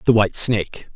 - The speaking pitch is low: Yes, low, 105 Hz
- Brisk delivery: No, average, 190 wpm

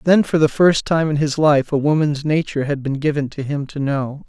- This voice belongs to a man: Yes, male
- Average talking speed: No, fast, 250 wpm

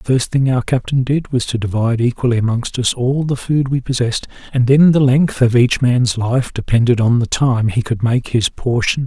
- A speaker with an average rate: No, fast, 230 wpm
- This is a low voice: Yes, low, 125 Hz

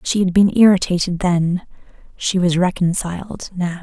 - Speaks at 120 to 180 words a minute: Yes, average, 140 wpm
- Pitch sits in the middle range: Yes, medium, 180 Hz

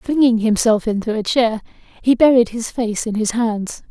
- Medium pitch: No, high, 230 Hz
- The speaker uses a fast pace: No, average, 185 wpm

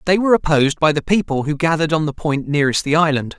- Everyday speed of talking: No, fast, 250 wpm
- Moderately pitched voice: Yes, medium, 155 Hz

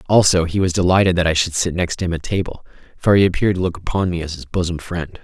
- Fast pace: Yes, fast, 265 wpm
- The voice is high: No, very low, 90 Hz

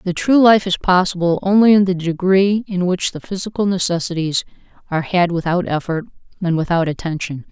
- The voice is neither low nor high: Yes, medium, 180 Hz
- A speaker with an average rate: Yes, average, 170 wpm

